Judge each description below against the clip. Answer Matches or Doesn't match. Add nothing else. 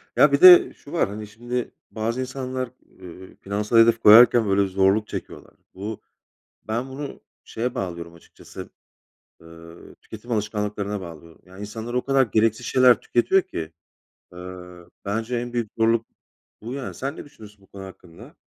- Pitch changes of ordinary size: Matches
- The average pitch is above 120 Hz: Doesn't match